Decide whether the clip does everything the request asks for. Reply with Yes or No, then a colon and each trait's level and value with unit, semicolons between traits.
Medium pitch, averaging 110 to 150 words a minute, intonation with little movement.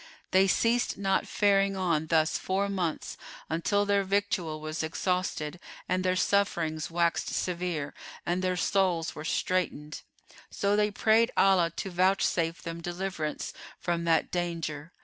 No: medium, 180 Hz; slow, 135 wpm; average, 3.0 semitones